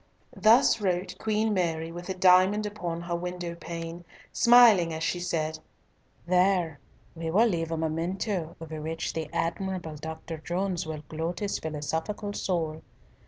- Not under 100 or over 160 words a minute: Yes, average, 145 wpm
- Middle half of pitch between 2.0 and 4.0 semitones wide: Yes, average, 2.7 semitones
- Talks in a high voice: No, medium, 170 Hz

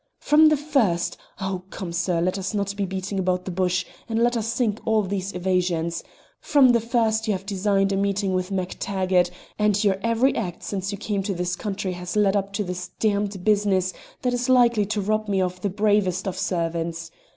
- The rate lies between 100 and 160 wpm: No, fast, 205 wpm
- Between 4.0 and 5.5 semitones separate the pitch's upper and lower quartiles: No, average, 2.7 semitones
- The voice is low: No, high, 195 Hz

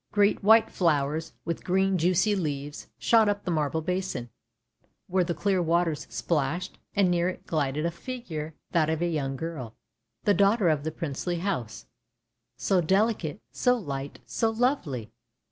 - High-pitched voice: No, medium, 170 Hz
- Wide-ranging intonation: No, average, 4.6 semitones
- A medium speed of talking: Yes, average, 160 wpm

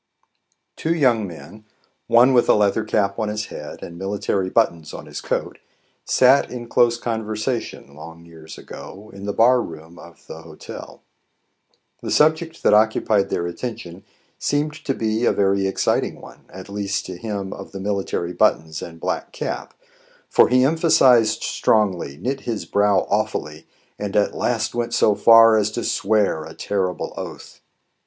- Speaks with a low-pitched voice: Yes, low, 105 Hz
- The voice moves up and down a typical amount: Yes, average, 4.1 semitones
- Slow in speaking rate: No, average, 160 wpm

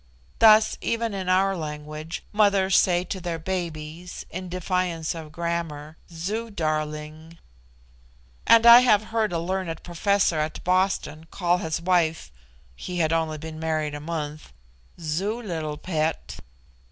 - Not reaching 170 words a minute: Yes, slow, 135 wpm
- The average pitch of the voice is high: No, medium, 170 Hz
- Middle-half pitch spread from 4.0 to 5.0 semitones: No, average, 3.3 semitones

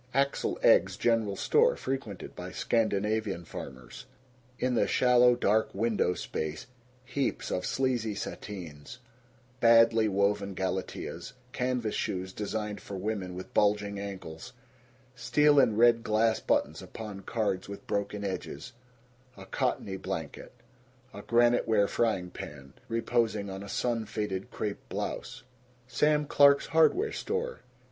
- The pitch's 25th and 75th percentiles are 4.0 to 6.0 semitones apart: No, average, 3.6 semitones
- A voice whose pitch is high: No, low, 110 Hz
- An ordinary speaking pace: No, slow, 125 wpm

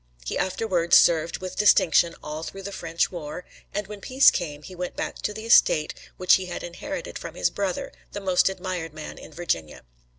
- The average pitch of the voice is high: No, medium, 180 Hz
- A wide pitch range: No, average, 3.0 semitones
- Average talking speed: Yes, average, 195 wpm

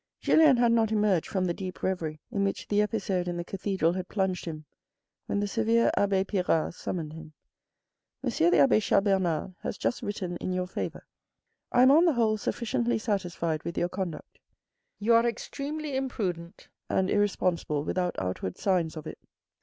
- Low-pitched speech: No, high, 190 Hz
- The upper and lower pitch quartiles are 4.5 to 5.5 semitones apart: No, average, 4.0 semitones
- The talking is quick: No, average, 175 wpm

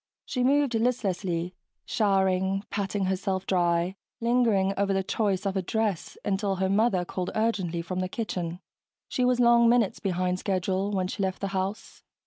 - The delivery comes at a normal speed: Yes, average, 160 wpm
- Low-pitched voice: No, high, 195 Hz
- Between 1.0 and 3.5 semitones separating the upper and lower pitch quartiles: Yes, average, 2.9 semitones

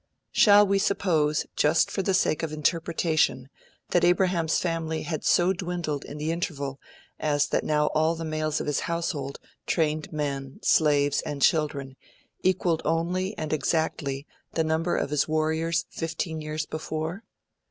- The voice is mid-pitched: Yes, medium, 160 Hz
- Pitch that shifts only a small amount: Yes, narrow, 2.1 semitones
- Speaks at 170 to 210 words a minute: No, average, 150 wpm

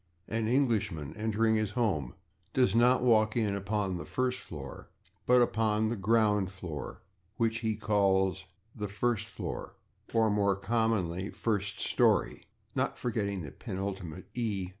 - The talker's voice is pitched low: Yes, low, 105 Hz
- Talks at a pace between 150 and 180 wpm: No, average, 140 wpm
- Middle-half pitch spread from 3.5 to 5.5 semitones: No, average, 2.9 semitones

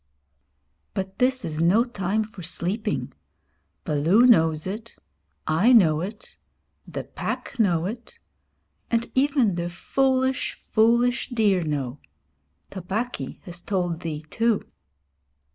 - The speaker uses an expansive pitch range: Yes, wide, 5.9 semitones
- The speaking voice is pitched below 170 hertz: No, high, 195 Hz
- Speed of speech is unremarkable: No, slow, 110 wpm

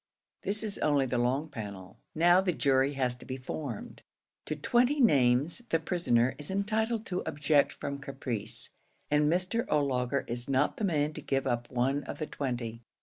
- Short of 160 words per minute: No, average, 175 wpm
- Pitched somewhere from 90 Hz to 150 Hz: Yes, medium, 140 Hz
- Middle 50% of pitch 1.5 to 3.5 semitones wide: No, average, 5.3 semitones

